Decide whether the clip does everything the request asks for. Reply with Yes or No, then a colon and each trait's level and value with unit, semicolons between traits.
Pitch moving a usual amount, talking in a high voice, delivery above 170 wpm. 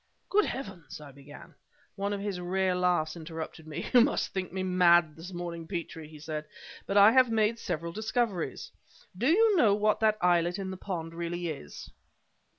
No: average, 3.9 semitones; medium, 180 Hz; average, 180 wpm